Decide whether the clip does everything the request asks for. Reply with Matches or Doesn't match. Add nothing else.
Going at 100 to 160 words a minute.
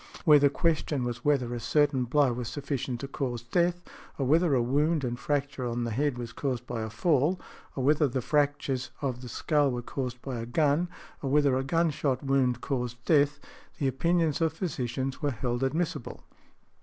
Doesn't match